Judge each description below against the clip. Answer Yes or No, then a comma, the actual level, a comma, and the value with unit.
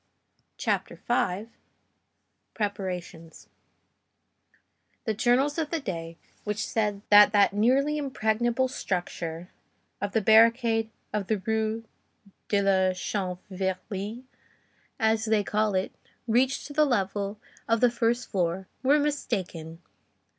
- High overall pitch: Yes, high, 215 Hz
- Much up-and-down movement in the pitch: No, average, 4.0 semitones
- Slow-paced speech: Yes, slow, 110 wpm